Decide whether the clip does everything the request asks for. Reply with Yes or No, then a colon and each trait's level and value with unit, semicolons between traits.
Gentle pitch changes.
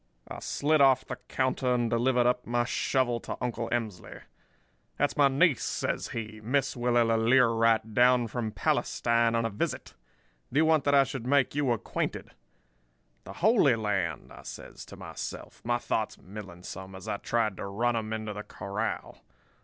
No: average, 3.0 semitones